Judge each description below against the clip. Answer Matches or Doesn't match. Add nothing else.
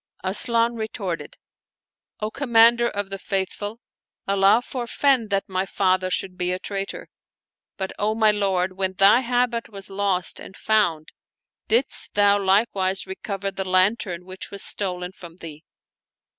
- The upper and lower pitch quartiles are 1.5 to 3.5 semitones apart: Matches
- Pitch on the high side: Matches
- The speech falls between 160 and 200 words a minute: Doesn't match